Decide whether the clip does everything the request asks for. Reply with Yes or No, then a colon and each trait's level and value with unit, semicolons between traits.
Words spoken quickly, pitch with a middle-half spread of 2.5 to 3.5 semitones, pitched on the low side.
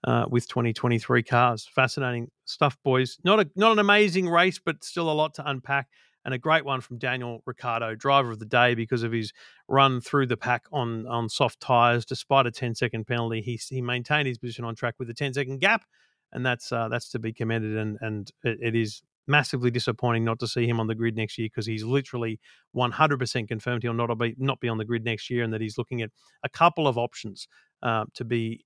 Yes: fast, 225 wpm; average, 2.8 semitones; low, 120 Hz